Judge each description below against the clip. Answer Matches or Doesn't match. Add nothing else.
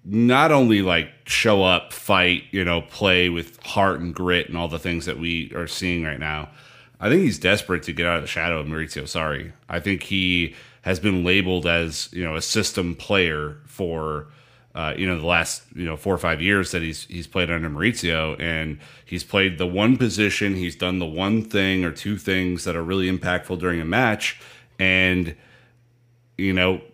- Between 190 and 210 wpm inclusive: Matches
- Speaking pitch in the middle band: Doesn't match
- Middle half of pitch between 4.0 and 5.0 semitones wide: Doesn't match